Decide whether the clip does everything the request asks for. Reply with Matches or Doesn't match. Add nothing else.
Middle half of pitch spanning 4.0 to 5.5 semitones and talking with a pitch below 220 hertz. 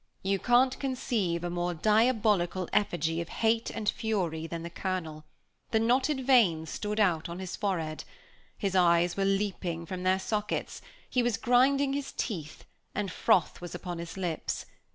Matches